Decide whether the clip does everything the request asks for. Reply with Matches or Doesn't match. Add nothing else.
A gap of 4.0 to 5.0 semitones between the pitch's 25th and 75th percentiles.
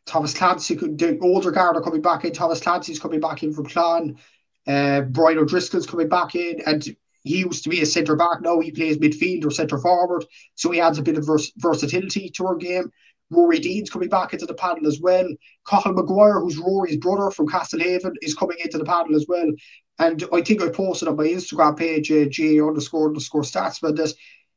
Doesn't match